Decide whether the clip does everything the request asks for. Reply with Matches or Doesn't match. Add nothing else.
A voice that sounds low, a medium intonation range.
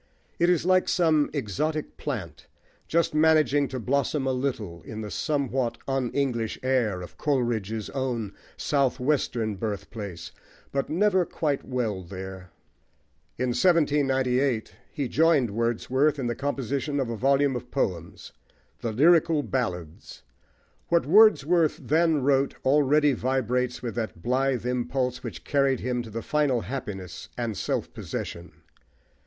Matches